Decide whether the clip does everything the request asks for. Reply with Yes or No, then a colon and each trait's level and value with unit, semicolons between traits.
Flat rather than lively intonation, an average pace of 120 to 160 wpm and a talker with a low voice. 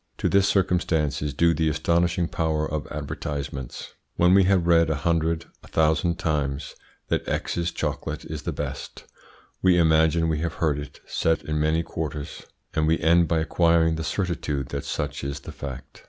No: narrow, 2.1 semitones; average, 175 wpm; very low, 80 Hz